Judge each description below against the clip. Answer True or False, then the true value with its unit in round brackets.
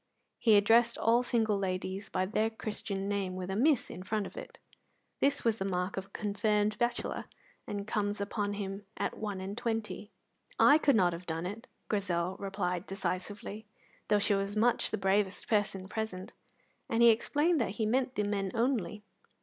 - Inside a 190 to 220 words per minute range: False (180 wpm)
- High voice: True (205 Hz)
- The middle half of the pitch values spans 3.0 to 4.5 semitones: False (2.5 semitones)